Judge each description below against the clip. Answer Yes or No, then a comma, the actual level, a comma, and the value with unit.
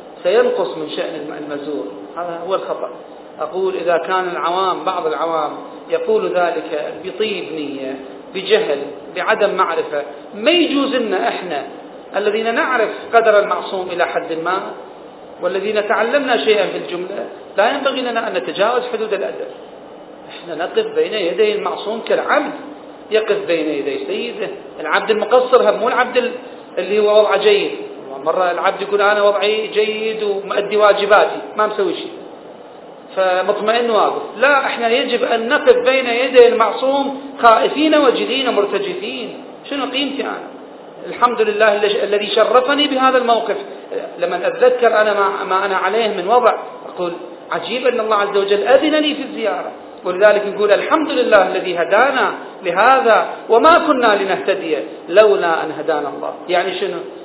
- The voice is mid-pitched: No, high, 220 Hz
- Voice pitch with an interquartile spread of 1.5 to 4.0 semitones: No, wide, 5.4 semitones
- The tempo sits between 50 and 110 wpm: No, fast, 135 wpm